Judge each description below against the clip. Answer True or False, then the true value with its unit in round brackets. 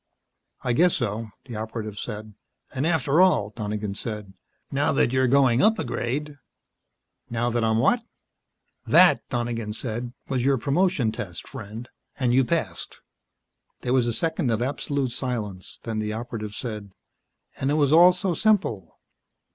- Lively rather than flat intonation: False (4.5 semitones)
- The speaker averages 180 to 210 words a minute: False (155 wpm)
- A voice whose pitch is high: False (120 Hz)